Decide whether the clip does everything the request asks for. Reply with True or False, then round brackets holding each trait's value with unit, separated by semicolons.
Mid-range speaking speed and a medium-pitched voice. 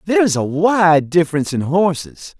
True (175 wpm; 175 Hz)